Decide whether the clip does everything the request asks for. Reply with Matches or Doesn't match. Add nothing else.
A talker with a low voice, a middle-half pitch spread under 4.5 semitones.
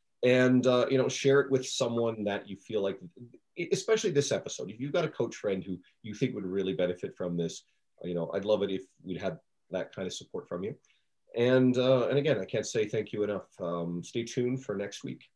Doesn't match